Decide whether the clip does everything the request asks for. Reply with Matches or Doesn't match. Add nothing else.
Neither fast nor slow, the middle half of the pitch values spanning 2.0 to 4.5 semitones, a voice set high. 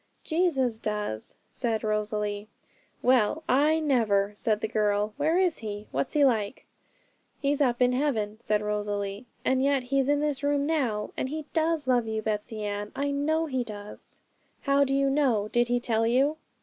Doesn't match